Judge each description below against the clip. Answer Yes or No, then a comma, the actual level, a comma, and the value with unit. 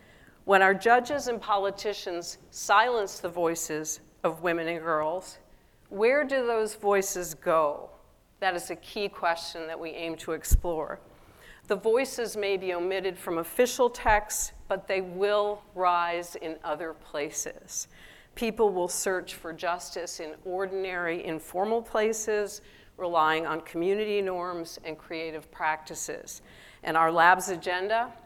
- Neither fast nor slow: No, slow, 130 wpm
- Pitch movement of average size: Yes, average, 3.9 semitones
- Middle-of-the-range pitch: Yes, medium, 180 Hz